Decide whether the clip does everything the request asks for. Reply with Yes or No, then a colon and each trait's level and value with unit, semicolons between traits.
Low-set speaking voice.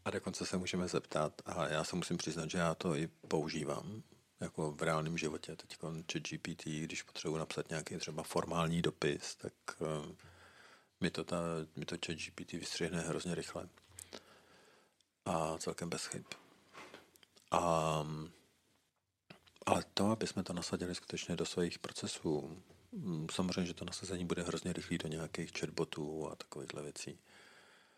Yes: very low, 85 Hz